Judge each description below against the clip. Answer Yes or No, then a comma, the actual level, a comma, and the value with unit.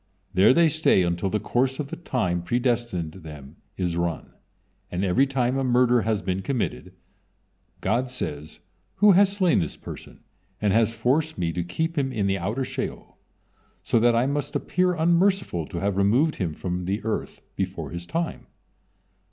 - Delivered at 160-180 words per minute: Yes, average, 170 wpm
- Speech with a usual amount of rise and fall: No, wide, 7.3 semitones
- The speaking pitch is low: Yes, low, 115 Hz